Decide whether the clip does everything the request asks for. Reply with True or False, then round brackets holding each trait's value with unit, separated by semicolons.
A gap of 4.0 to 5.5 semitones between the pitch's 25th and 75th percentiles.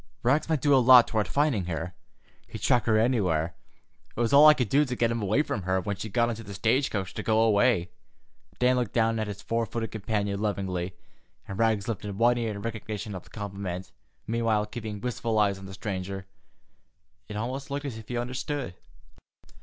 False (3.4 semitones)